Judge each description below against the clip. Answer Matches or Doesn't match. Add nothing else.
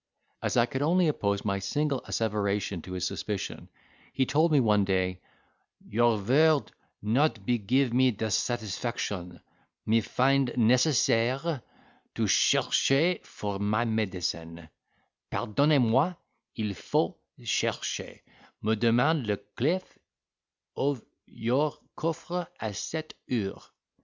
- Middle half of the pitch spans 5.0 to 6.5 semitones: Matches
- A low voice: Matches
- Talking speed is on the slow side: Matches